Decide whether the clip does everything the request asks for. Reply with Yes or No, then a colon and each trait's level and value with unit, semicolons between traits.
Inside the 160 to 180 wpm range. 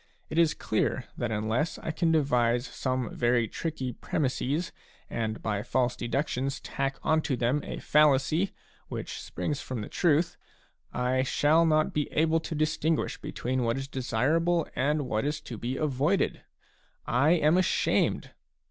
No: average, 150 wpm